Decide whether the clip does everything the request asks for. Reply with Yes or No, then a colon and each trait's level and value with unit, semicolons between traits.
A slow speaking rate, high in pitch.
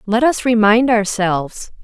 Yes: slow, 130 wpm; high, 220 Hz